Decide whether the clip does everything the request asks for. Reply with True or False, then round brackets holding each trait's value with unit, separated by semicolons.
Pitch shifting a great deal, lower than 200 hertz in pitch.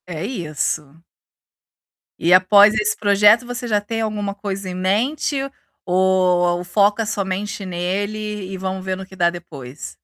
False (2.6 semitones; 190 Hz)